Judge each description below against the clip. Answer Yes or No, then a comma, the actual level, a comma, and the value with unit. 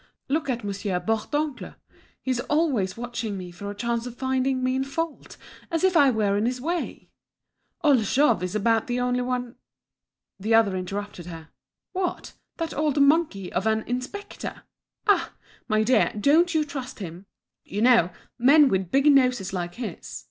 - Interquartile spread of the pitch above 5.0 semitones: Yes, wide, 5.6 semitones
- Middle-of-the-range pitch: No, high, 245 Hz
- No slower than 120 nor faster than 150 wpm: No, average, 165 wpm